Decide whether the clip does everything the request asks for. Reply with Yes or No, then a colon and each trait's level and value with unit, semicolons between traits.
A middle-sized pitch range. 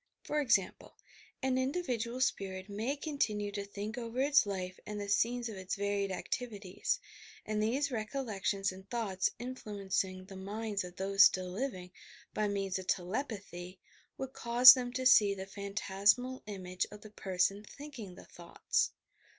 Yes: average, 4.3 semitones